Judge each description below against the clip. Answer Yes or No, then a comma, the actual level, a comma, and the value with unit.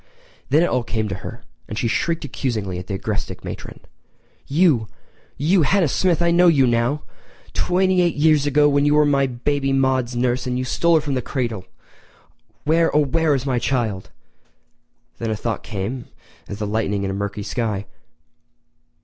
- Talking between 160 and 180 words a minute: Yes, average, 165 wpm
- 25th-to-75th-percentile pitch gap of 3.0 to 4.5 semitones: No, average, 5.1 semitones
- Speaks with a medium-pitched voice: No, low, 130 Hz